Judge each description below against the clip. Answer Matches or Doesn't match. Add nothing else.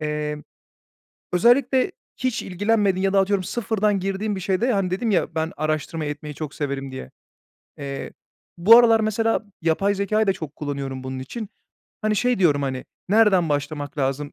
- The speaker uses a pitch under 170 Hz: Doesn't match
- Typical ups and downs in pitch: Doesn't match